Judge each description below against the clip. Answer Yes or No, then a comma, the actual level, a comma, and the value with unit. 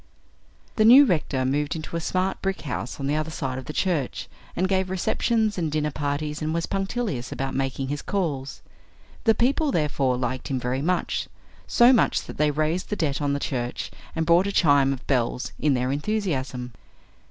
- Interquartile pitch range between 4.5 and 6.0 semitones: Yes, wide, 5.6 semitones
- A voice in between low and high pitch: Yes, medium, 150 Hz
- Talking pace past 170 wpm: Yes, average, 190 wpm